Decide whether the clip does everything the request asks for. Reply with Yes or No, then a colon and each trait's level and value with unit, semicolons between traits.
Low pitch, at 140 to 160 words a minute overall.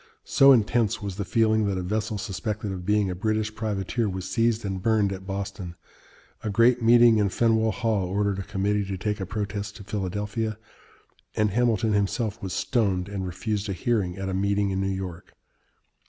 No: low, 105 Hz; average, 185 wpm